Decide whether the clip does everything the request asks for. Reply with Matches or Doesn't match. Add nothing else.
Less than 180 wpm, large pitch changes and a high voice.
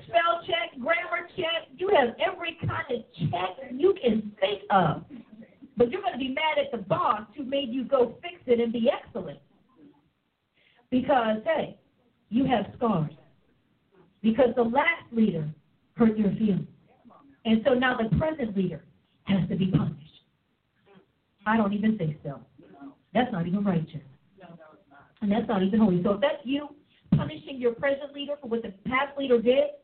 Matches